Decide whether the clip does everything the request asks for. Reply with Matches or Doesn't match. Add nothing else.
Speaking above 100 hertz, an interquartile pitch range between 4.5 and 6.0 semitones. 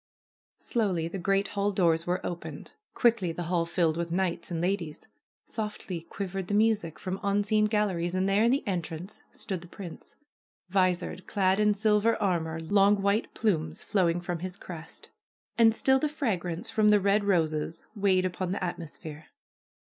Doesn't match